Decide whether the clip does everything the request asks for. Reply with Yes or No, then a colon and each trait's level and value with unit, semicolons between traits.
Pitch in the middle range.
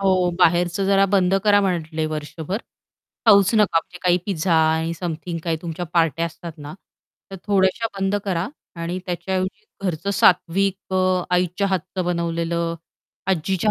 Yes: medium, 180 Hz